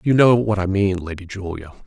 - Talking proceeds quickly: Yes, fast, 225 wpm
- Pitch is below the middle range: Yes, low, 100 Hz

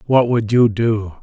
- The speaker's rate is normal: Yes, average, 195 wpm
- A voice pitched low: Yes, low, 115 Hz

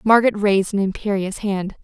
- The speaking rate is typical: Yes, average, 165 wpm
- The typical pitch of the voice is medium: No, high, 200 Hz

